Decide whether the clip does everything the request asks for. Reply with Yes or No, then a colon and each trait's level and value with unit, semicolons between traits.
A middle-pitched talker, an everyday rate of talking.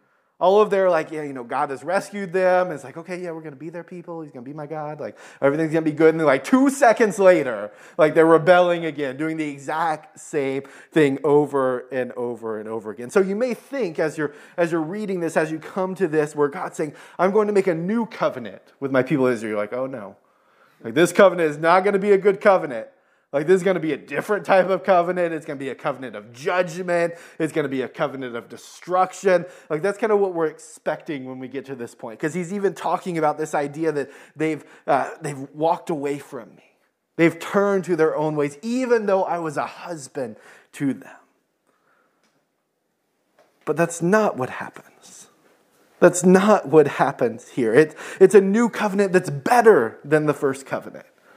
No: medium, 160 Hz; fast, 215 wpm